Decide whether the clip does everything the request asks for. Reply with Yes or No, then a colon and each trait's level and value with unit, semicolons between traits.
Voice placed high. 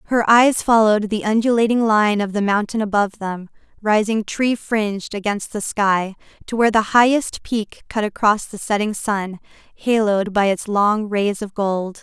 Yes: high, 210 Hz